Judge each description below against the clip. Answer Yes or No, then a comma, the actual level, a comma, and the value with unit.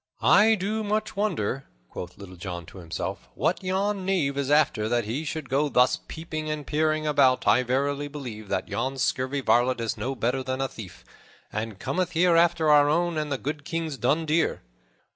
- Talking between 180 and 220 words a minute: Yes, average, 190 wpm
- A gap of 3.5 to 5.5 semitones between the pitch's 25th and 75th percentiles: Yes, average, 4.6 semitones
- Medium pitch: Yes, medium, 145 Hz